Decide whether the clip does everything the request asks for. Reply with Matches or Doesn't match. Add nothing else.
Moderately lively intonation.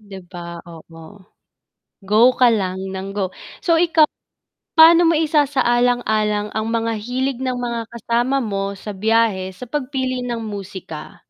Matches